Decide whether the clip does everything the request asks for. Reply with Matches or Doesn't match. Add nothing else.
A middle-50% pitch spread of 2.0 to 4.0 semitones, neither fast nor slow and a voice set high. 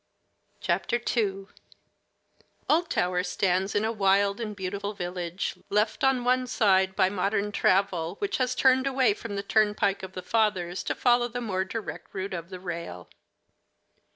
Matches